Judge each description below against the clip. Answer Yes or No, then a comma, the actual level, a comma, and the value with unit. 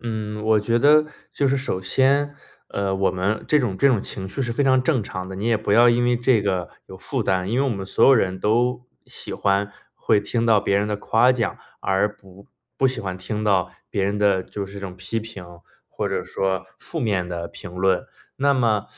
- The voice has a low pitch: Yes, low, 105 Hz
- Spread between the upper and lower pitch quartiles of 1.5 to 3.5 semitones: No, average, 4.1 semitones